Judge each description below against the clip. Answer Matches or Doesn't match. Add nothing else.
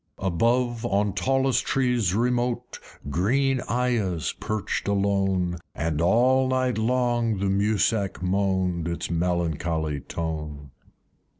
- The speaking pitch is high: Doesn't match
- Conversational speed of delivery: Doesn't match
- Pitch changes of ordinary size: Doesn't match